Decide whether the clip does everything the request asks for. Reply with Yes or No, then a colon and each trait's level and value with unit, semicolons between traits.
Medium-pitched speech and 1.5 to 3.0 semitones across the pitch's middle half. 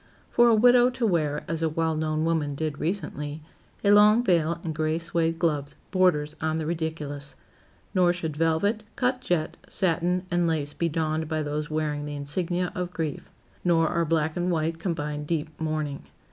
Yes: medium, 160 Hz; narrow, 2.5 semitones